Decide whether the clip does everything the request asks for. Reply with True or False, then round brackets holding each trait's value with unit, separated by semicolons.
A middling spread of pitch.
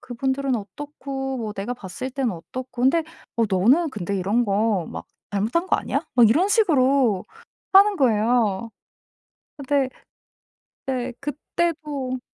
True (4.7 semitones)